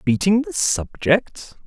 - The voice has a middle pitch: Yes, medium, 160 Hz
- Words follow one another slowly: Yes, slow, 110 wpm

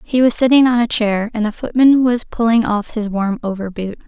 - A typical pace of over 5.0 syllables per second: Yes, 5.2 syllables/s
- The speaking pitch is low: No, high, 225 Hz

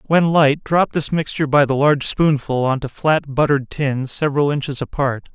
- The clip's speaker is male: Yes, male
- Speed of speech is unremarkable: Yes, average, 190 wpm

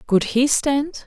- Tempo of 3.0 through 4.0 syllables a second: Yes, 3.2 syllables/s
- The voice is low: No, very high, 260 Hz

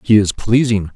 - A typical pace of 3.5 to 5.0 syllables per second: Yes, 4.8 syllables/s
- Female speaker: No, male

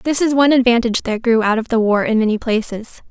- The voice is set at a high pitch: Yes, high, 235 Hz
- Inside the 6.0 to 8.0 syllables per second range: Yes, 6.5 syllables/s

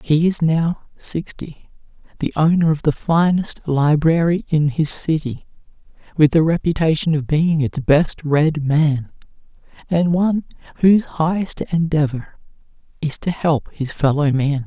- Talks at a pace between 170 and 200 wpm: No, slow, 135 wpm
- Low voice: No, medium, 155 Hz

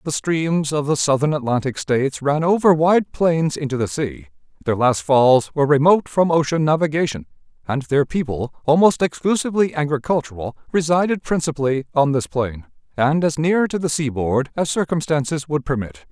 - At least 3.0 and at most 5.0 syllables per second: No, 5.3 syllables/s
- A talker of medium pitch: Yes, medium, 145 Hz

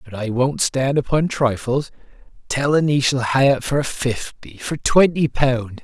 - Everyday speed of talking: Yes, average, 145 wpm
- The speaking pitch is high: No, low, 130 Hz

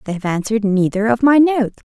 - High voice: Yes, high, 225 Hz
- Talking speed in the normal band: No, fast, 215 wpm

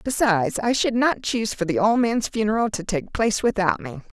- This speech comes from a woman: Yes, female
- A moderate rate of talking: No, fast, 215 wpm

